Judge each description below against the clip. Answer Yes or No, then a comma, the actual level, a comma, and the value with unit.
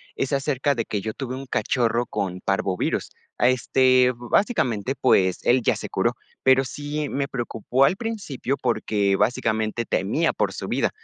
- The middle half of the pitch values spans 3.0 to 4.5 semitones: Yes, average, 3.8 semitones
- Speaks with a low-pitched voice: Yes, low, 125 Hz